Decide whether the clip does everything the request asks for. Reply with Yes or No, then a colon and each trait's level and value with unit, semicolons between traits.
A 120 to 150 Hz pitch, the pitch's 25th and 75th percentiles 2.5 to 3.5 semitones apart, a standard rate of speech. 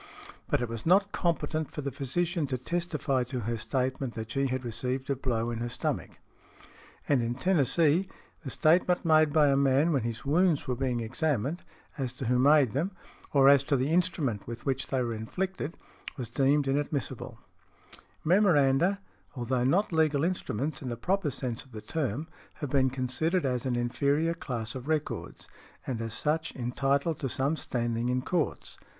No: low, 135 Hz; average, 4.2 semitones; average, 175 wpm